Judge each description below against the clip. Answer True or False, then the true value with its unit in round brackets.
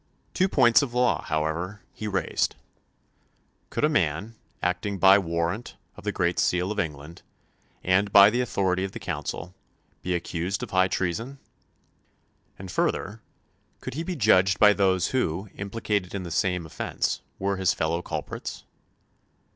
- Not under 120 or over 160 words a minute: True (150 wpm)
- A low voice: True (95 Hz)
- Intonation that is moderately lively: True (3.1 semitones)